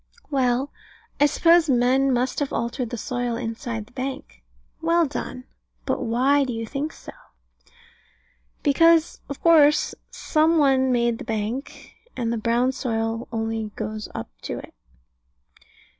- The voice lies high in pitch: Yes, very high, 250 Hz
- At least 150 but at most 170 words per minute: No, average, 140 wpm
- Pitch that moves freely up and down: No, average, 3.8 semitones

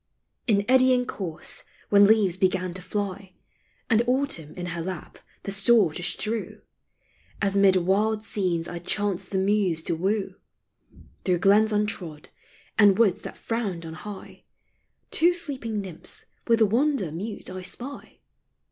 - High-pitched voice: Yes, high, 200 Hz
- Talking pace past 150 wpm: No, average, 145 wpm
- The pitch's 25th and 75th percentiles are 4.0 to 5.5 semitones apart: No, average, 3.3 semitones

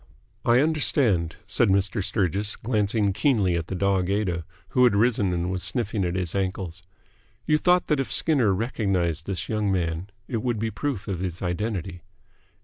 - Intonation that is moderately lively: Yes, average, 4.0 semitones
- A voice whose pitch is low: Yes, low, 100 Hz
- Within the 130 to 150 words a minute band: No, average, 170 wpm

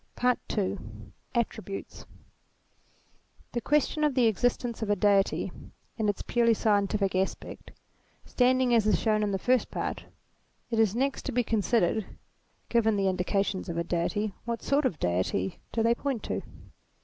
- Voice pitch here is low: No, high, 220 Hz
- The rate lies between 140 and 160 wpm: Yes, average, 155 wpm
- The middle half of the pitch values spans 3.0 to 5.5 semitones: Yes, average, 3.5 semitones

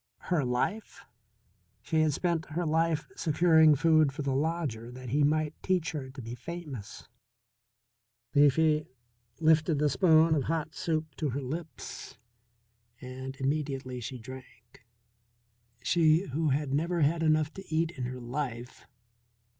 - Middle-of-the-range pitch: Yes, medium, 150 Hz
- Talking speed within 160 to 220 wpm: No, average, 140 wpm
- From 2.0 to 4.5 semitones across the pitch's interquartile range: Yes, average, 3.5 semitones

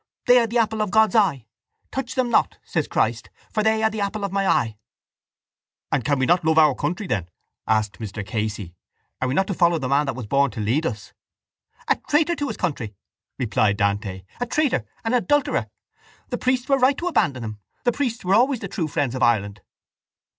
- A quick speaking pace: Yes, fast, 210 wpm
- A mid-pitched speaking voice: Yes, medium, 165 Hz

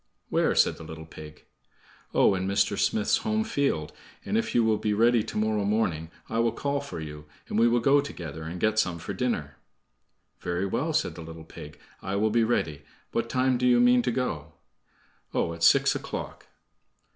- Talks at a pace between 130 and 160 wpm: No, average, 195 wpm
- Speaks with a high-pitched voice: No, low, 105 Hz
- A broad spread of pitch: Yes, wide, 7.0 semitones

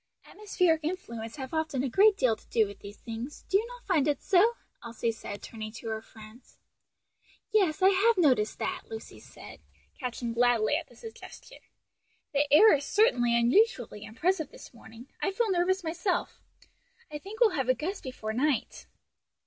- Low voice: No, very high, 290 Hz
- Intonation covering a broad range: Yes, wide, 8.5 semitones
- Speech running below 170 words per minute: No, average, 175 wpm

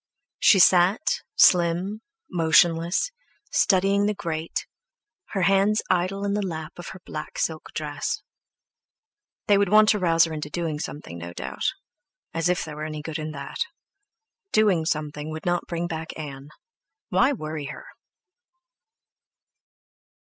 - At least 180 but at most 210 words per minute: No, average, 140 wpm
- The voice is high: No, medium, 170 Hz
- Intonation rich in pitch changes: No, average, 3.9 semitones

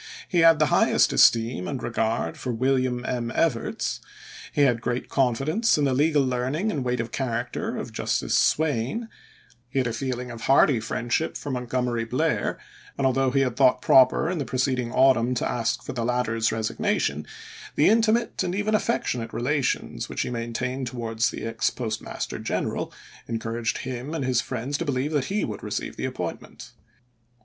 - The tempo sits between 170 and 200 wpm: Yes, average, 180 wpm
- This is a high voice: No, low, 125 Hz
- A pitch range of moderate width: Yes, average, 3.2 semitones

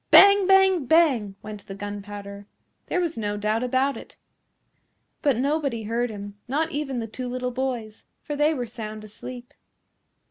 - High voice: Yes, high, 245 Hz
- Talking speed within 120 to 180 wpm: Yes, average, 155 wpm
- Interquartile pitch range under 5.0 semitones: No, average, 5.3 semitones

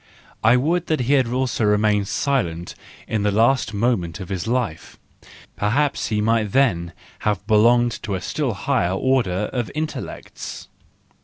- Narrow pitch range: No, average, 4.3 semitones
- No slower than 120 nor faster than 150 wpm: Yes, average, 145 wpm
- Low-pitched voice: Yes, low, 110 Hz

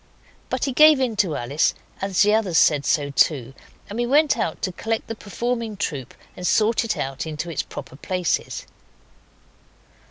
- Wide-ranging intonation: Yes, wide, 7.2 semitones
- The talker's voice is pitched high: Yes, high, 195 Hz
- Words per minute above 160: Yes, average, 170 wpm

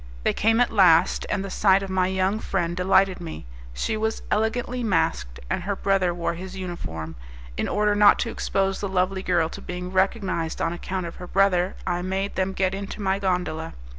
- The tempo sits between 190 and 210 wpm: Yes, average, 195 wpm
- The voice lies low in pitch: No, high, 190 Hz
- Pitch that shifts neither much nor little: No, narrow, 1.9 semitones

